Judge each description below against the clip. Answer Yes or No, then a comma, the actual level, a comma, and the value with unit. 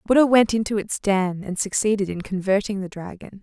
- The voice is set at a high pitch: Yes, high, 200 Hz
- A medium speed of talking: Yes, average, 195 wpm